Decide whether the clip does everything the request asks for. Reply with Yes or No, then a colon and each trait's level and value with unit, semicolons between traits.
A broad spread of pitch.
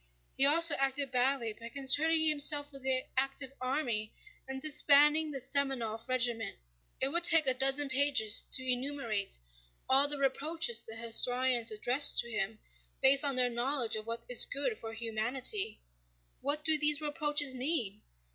No: average, 3.5 semitones